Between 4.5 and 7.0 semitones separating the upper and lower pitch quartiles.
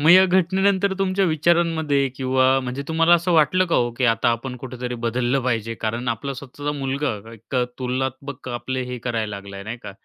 Yes: average, 5.2 semitones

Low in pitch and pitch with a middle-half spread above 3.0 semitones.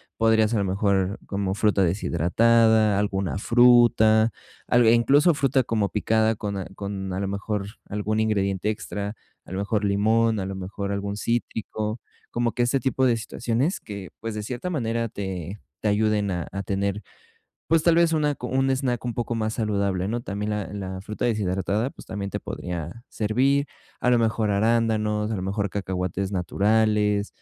No: low, 105 Hz; average, 2.7 semitones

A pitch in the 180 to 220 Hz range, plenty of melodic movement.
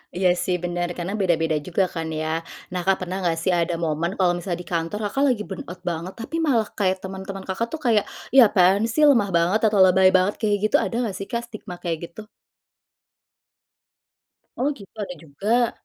No: high, 190 Hz; average, 3.1 semitones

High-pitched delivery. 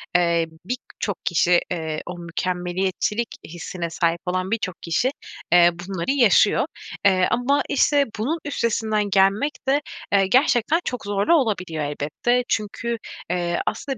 Yes: high, 195 Hz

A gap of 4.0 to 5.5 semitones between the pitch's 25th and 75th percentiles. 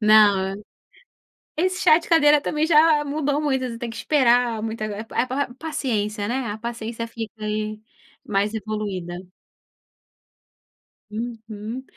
Yes: average, 4.9 semitones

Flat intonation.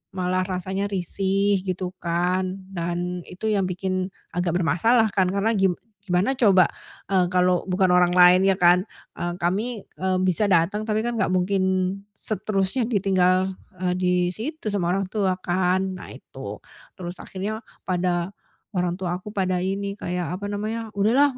Yes: narrow, 1.8 semitones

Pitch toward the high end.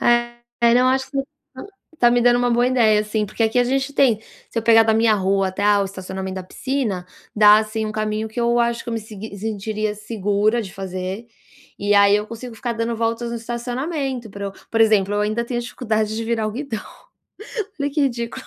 Yes: high, 225 Hz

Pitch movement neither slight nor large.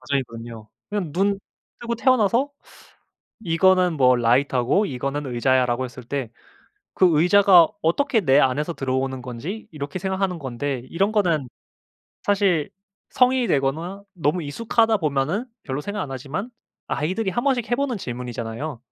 No: wide, 7.3 semitones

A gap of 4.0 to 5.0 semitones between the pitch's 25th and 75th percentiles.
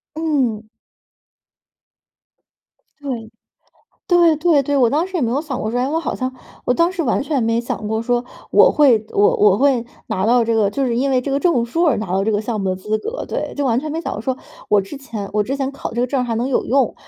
Yes: average, 4.3 semitones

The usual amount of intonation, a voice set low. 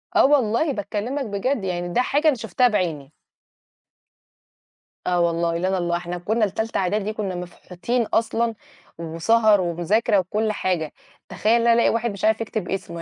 No: average, 4.6 semitones; high, 205 Hz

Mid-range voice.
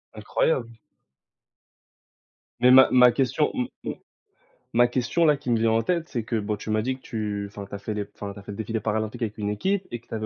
No: low, 115 Hz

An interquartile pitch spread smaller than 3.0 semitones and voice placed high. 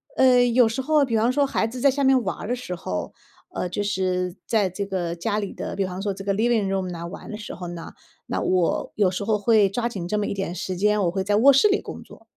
No: average, 4.2 semitones; high, 205 Hz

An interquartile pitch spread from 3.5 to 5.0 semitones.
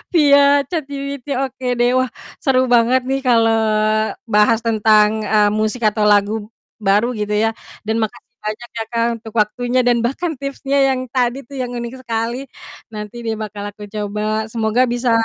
No: average, 3.0 semitones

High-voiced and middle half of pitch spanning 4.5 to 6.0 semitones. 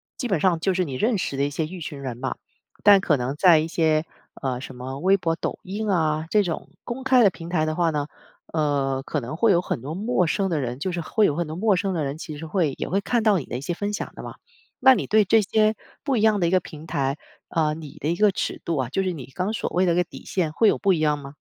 No: medium, 170 Hz; average, 4.8 semitones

